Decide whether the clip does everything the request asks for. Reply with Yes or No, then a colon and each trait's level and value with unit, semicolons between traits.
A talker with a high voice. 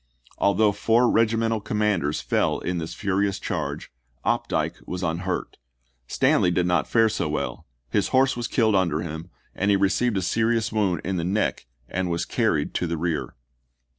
No: very low, 95 Hz